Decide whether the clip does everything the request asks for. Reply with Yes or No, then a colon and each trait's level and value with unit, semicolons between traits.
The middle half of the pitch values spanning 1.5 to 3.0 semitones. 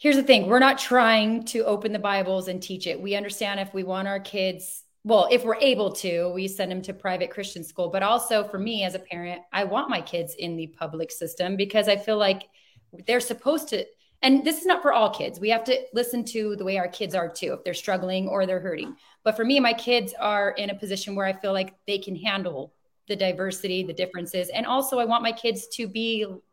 No: average, 3.6 semitones